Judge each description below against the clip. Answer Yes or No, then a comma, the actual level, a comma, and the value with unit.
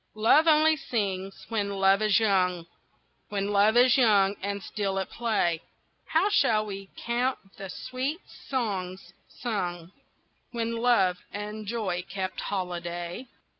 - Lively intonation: No, average, 3.8 semitones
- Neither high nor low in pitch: No, high, 205 Hz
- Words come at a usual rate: No, slow, 130 wpm